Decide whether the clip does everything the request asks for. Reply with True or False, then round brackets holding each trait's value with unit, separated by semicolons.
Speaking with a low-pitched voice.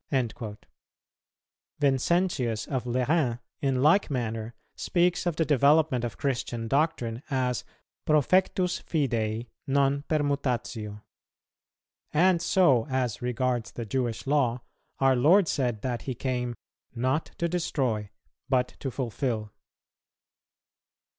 True (130 Hz)